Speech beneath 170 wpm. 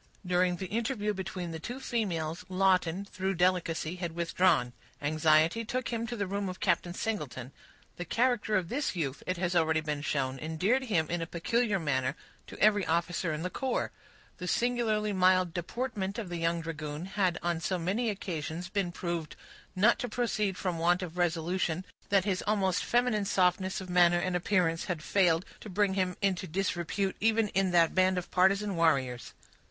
No: average, 180 wpm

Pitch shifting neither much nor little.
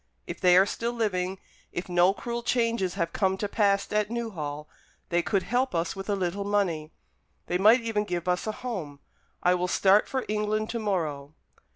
Yes: average, 3.5 semitones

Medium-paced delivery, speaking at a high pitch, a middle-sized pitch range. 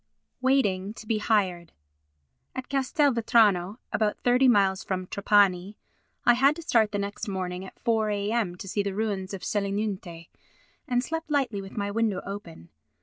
Yes: average, 155 wpm; high, 205 Hz; average, 3.6 semitones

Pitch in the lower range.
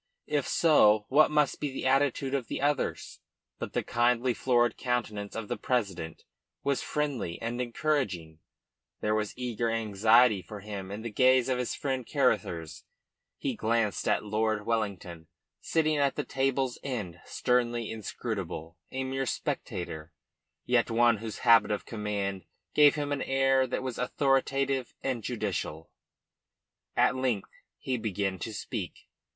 Yes: low, 120 Hz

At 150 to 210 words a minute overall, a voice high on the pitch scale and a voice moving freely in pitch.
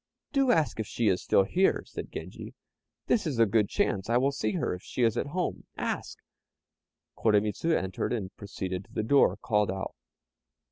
No: average, 185 wpm; low, 110 Hz; wide, 5.9 semitones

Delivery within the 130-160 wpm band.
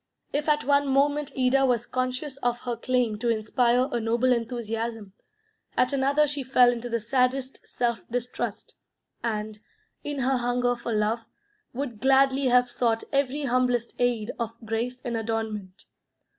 Yes: average, 150 wpm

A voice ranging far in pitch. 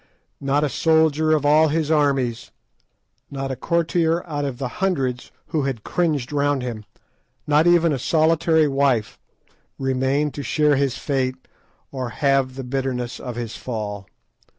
No: average, 3.3 semitones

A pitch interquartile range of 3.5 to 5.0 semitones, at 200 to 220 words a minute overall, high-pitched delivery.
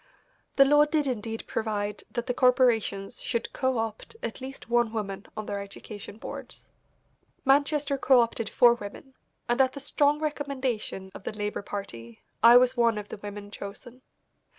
No: average, 4.2 semitones; average, 165 wpm; high, 235 Hz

